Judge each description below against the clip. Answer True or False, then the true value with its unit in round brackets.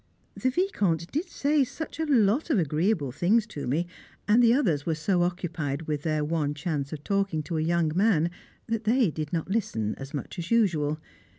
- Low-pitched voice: False (170 Hz)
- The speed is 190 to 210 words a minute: True (195 wpm)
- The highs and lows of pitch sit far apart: True (6.4 semitones)